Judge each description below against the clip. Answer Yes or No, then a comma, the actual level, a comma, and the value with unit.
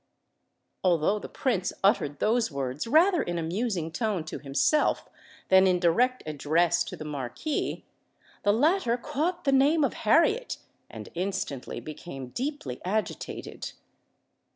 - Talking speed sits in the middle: No, slow, 130 wpm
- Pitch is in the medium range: No, high, 195 Hz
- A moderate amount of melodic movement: No, wide, 8.9 semitones